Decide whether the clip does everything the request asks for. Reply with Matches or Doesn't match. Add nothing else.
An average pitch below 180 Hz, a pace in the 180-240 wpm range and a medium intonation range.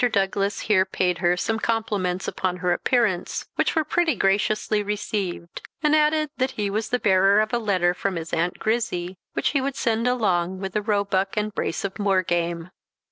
Doesn't match